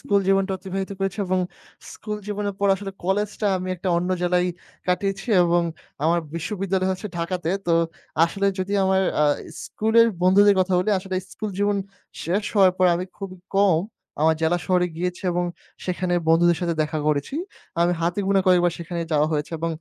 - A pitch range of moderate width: No, narrow, 2.3 semitones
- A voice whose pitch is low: No, medium, 185 Hz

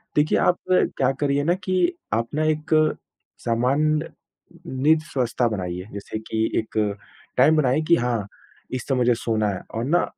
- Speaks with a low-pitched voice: Yes, low, 130 Hz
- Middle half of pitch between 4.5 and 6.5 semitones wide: Yes, wide, 5.4 semitones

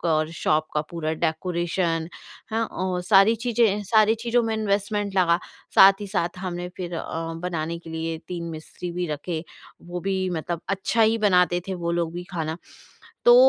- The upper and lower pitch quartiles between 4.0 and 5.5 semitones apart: No, average, 3.3 semitones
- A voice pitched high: No, medium, 180 Hz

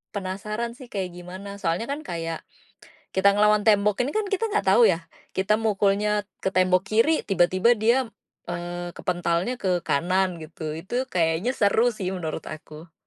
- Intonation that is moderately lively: Yes, average, 3.4 semitones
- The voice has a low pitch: No, high, 190 Hz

